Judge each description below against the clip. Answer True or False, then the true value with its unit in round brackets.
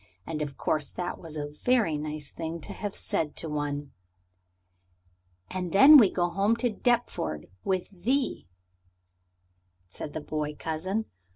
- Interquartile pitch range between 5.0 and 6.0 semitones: True (5.4 semitones)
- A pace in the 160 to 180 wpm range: False (145 wpm)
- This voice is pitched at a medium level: True (165 Hz)